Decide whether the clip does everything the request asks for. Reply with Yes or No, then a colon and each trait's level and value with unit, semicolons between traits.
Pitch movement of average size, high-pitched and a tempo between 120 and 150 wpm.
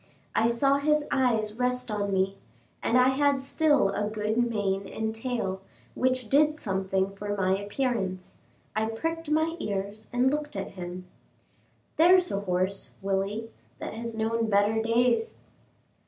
Yes: average, 4.8 semitones; high, 225 Hz; average, 140 wpm